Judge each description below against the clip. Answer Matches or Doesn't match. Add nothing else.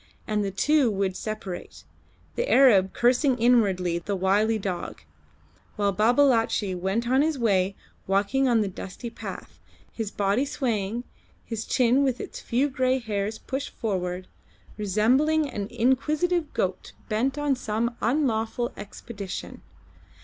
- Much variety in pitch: Doesn't match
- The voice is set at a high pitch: Matches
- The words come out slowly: Matches